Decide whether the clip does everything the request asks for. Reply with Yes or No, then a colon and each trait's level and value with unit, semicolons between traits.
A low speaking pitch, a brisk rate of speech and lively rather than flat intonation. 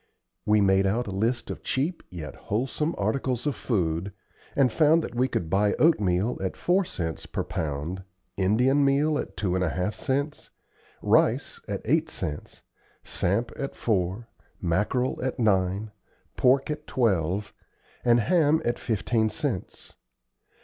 No: low, 110 Hz; average, 145 wpm; wide, 6.0 semitones